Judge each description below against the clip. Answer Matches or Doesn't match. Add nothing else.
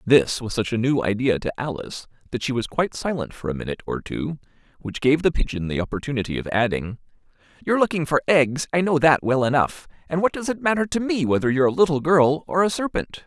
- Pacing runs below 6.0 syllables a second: Doesn't match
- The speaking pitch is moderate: Matches